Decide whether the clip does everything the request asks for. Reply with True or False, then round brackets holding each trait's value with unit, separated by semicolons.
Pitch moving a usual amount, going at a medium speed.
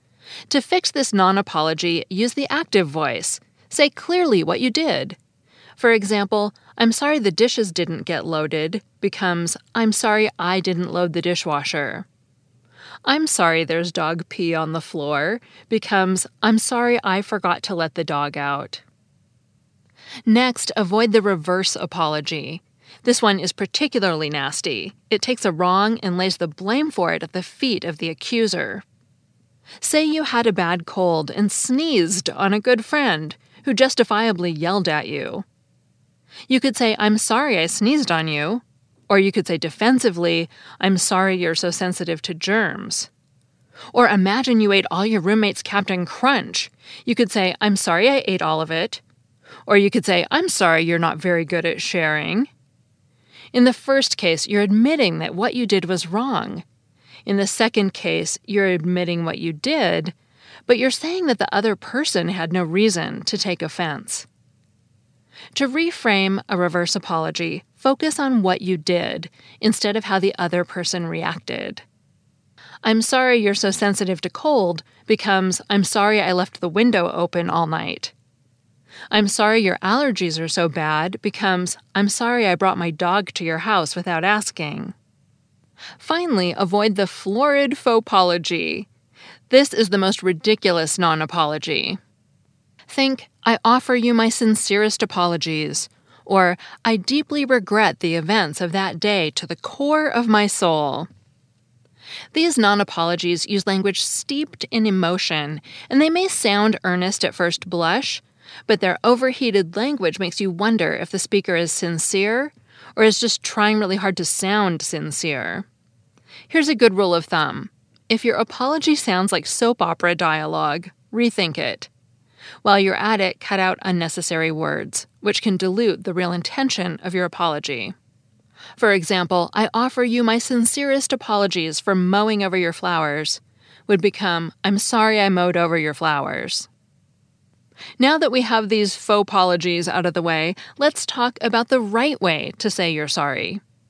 True (4.8 semitones; 155 wpm)